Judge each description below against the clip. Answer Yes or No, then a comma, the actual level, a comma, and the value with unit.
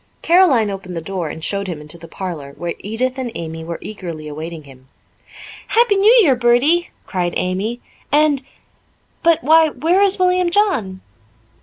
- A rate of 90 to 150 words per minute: No, average, 160 wpm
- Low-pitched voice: No, high, 215 Hz